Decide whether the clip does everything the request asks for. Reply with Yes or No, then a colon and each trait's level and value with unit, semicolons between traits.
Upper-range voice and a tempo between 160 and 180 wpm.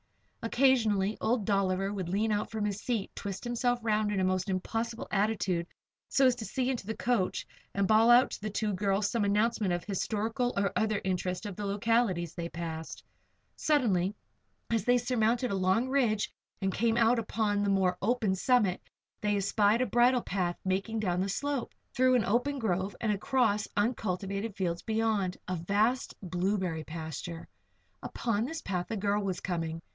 Yes: high, 205 Hz; average, 175 wpm